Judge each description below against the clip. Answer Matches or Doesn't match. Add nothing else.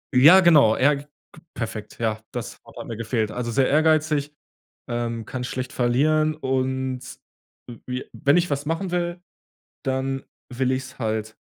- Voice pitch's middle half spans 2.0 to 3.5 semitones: Doesn't match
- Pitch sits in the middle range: Doesn't match